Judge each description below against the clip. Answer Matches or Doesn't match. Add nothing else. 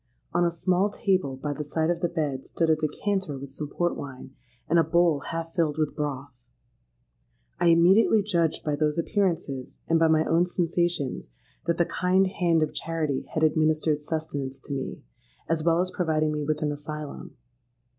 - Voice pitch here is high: Doesn't match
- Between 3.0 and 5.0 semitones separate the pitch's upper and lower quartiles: Doesn't match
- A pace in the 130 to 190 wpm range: Matches